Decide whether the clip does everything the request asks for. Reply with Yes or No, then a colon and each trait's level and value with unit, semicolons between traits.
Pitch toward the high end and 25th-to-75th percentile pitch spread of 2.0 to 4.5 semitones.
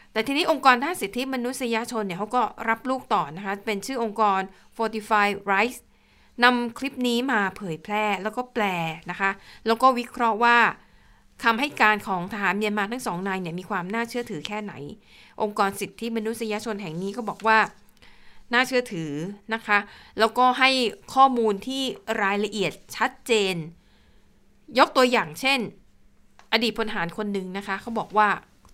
Yes: high, 215 Hz; average, 3.4 semitones